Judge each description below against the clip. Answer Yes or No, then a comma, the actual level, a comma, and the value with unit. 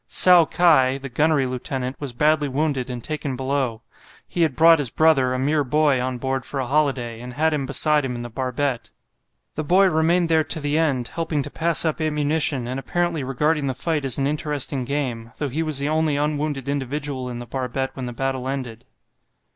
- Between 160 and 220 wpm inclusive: Yes, fast, 205 wpm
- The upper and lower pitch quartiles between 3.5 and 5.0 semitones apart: No, average, 3.1 semitones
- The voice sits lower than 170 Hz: Yes, medium, 140 Hz